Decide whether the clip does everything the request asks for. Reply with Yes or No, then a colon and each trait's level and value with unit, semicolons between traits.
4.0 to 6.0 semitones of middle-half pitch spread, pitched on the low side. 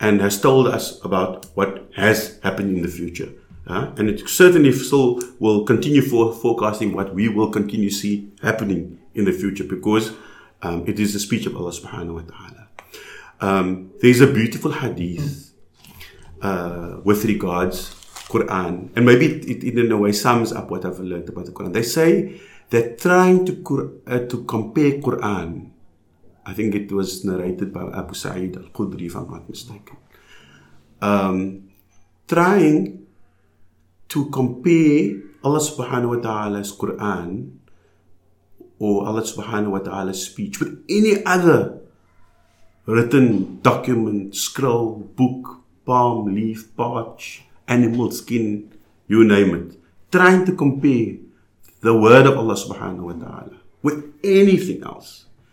Yes: average, 4.4 semitones; low, 105 Hz